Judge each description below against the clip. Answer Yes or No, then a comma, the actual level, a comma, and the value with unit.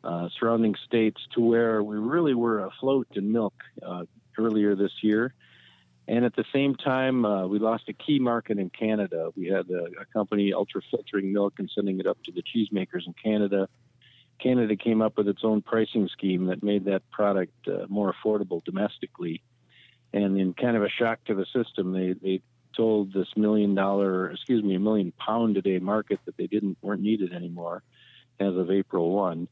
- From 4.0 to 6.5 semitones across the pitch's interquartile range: No, average, 2.9 semitones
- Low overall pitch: Yes, low, 105 Hz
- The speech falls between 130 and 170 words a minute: No, average, 185 wpm